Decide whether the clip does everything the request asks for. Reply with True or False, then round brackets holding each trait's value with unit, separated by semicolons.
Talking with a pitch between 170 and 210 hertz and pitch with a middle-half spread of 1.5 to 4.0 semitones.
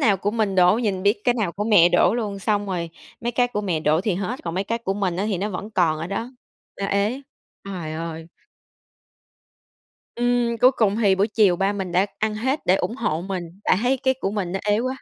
True (200 Hz; 3.7 semitones)